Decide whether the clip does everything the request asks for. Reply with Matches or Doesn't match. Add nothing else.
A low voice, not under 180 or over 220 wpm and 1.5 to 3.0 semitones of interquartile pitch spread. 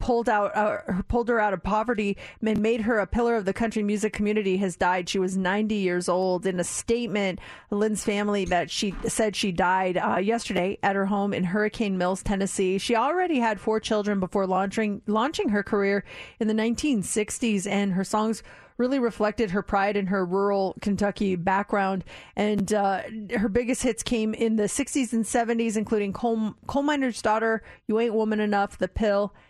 Doesn't match